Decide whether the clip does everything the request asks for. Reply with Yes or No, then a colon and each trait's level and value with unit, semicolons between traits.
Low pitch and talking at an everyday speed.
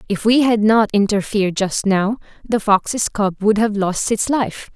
No: high, 210 Hz; average, 190 wpm